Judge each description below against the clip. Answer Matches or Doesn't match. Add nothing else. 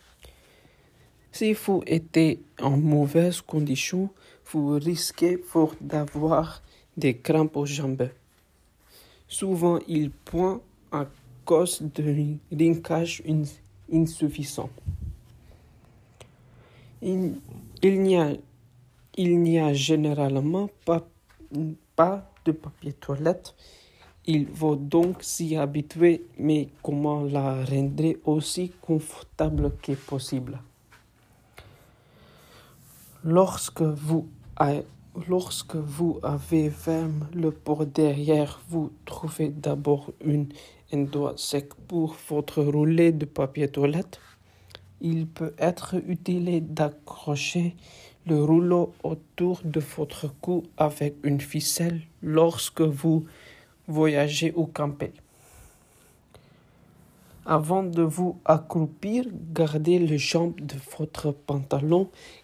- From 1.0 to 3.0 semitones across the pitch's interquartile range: Matches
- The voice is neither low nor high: Matches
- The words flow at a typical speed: Doesn't match